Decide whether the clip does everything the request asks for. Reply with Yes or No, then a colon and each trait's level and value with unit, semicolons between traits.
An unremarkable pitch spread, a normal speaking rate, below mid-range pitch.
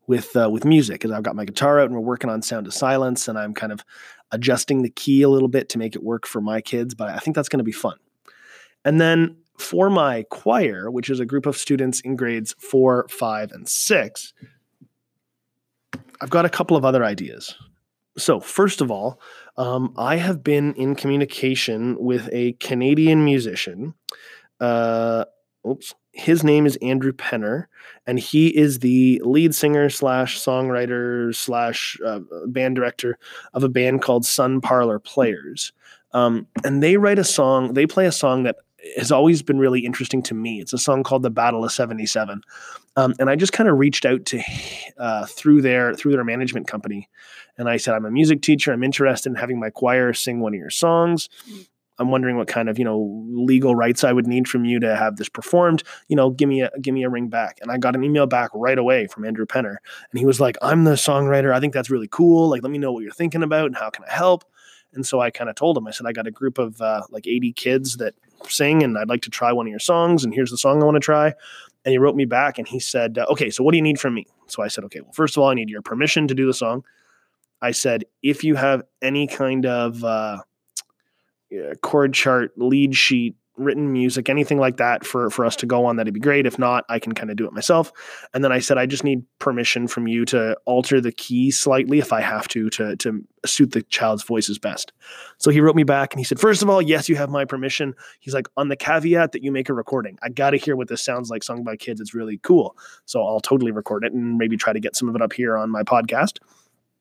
No: average, 3.3 semitones; fast, 235 wpm; low, 130 Hz